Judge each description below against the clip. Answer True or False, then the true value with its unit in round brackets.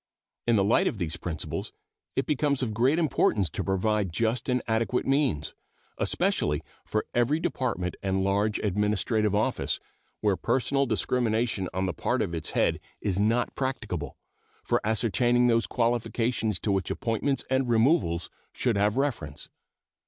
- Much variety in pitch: False (4.3 semitones)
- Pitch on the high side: False (110 Hz)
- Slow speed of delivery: False (145 wpm)